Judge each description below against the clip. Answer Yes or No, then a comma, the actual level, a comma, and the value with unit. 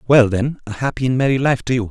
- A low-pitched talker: Yes, low, 125 Hz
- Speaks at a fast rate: Yes, fast, 285 wpm